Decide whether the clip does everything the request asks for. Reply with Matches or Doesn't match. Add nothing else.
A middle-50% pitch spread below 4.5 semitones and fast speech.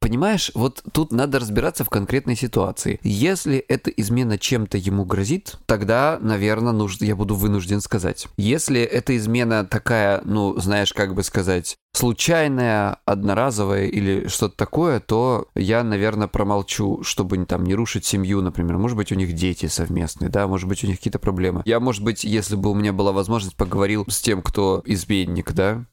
Matches